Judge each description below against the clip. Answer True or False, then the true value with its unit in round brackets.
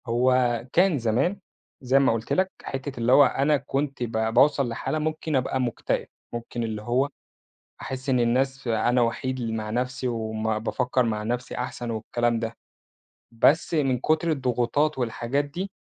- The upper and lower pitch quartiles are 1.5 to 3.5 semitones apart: True (3.0 semitones)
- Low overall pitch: True (125 Hz)